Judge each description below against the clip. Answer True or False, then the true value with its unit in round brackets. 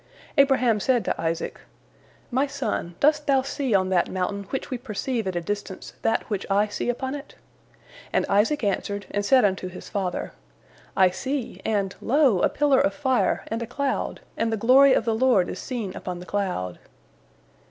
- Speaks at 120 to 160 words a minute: False (185 wpm)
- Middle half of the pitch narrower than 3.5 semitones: False (5.6 semitones)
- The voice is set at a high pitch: True (225 Hz)